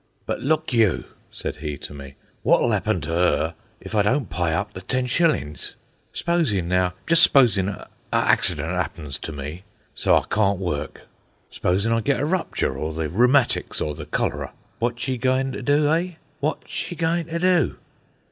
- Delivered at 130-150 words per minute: No, average, 175 wpm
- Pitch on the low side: Yes, low, 105 Hz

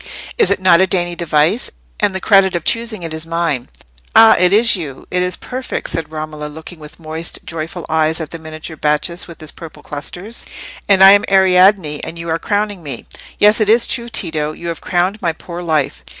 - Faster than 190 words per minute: Yes, fast, 205 wpm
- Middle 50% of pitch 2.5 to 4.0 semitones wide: Yes, average, 3.5 semitones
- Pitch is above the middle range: No, medium, 170 Hz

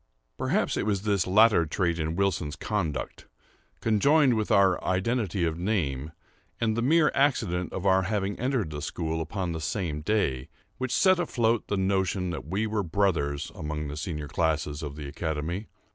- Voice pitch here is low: Yes, very low, 95 Hz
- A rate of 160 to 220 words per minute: Yes, average, 170 wpm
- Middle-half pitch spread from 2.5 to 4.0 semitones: No, average, 5.3 semitones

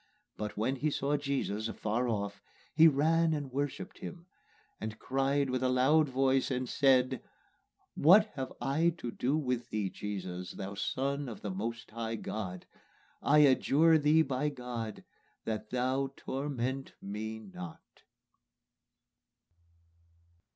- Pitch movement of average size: Yes, average, 4.5 semitones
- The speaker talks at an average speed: No, slow, 130 wpm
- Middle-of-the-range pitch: No, low, 130 Hz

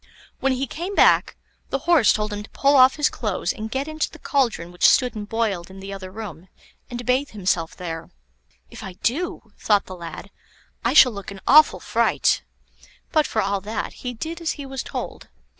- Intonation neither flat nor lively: No, wide, 5.8 semitones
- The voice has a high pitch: Yes, high, 220 Hz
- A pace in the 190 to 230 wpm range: Yes, average, 200 wpm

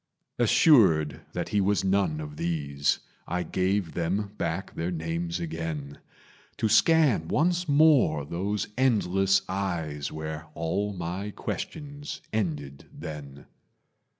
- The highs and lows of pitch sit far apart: No, average, 4.8 semitones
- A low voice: Yes, very low, 90 Hz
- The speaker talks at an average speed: No, slow, 115 wpm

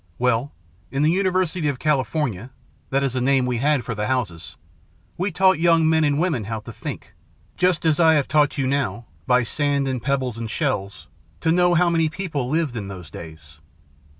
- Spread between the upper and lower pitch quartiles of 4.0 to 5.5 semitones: Yes, average, 4.8 semitones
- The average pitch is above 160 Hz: No, medium, 140 Hz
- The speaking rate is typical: Yes, average, 195 wpm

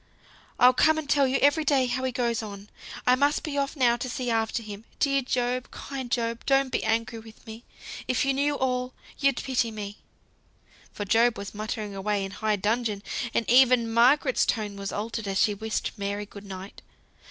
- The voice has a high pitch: Yes, high, 235 Hz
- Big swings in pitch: No, average, 3.6 semitones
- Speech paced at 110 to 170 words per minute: No, average, 195 wpm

